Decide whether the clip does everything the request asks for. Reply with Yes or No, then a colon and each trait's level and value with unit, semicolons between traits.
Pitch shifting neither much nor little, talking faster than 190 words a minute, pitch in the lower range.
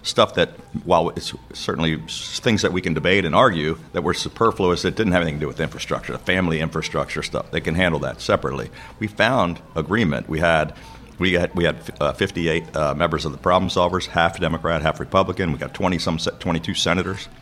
No: narrow, 2.3 semitones; fast, 205 wpm; very low, 85 Hz